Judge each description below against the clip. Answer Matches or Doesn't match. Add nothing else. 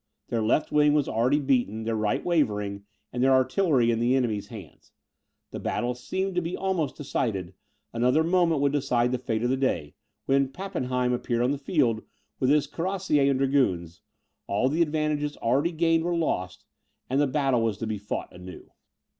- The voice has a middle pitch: Doesn't match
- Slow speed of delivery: Doesn't match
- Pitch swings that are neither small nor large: Matches